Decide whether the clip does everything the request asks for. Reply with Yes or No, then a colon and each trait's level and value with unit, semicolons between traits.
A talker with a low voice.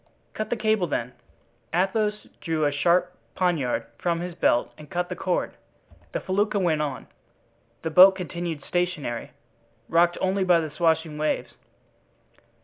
No: medium, 175 Hz